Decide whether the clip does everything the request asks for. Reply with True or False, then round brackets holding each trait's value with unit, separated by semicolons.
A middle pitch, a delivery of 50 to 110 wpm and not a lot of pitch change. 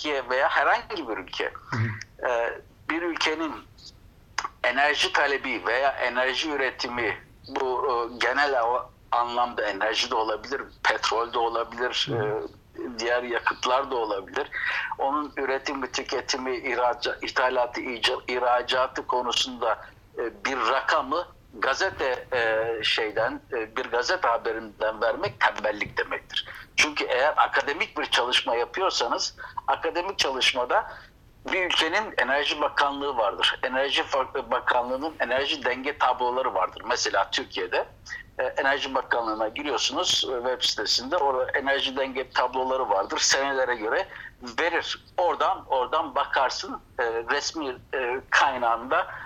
False (125 Hz; 100 wpm; 2.0 semitones)